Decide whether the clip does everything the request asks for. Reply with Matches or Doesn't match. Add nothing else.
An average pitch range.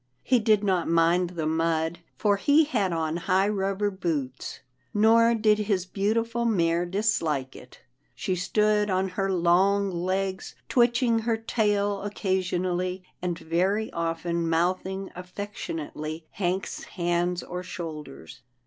Matches